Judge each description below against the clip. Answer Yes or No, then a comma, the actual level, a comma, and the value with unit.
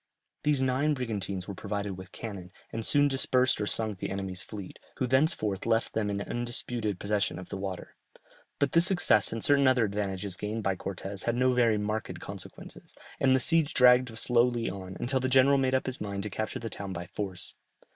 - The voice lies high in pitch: No, low, 110 Hz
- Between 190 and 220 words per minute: Yes, average, 195 wpm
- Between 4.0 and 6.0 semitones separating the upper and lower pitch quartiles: Yes, average, 4.5 semitones